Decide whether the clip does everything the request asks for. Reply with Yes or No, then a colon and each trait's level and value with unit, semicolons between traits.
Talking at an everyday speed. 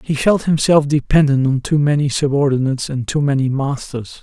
Yes: average, 170 wpm